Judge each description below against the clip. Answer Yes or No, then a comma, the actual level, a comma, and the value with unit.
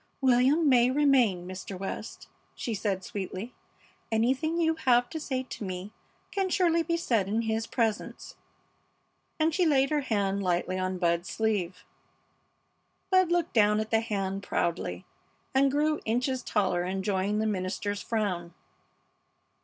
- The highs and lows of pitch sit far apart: Yes, wide, 6.0 semitones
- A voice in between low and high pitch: No, high, 220 Hz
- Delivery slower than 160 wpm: Yes, average, 140 wpm